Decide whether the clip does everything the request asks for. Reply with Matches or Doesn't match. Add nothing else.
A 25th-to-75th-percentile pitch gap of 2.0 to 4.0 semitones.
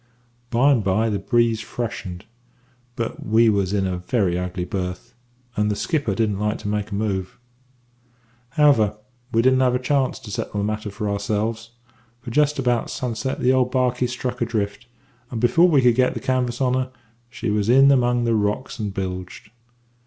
Matches